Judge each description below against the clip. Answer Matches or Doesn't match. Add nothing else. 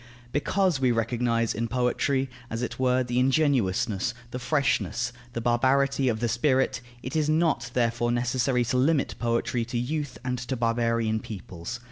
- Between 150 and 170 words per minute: Matches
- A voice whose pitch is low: Matches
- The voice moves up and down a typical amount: Doesn't match